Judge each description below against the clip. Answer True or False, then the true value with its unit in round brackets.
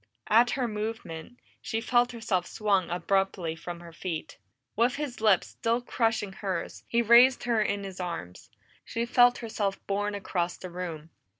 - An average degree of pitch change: True (4.7 semitones)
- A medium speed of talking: True (160 wpm)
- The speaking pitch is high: True (205 Hz)